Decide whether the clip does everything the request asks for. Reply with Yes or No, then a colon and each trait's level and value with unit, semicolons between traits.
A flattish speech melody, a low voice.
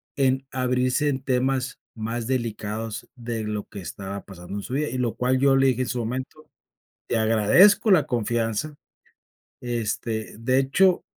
No: average, 3.2 semitones; low, 125 Hz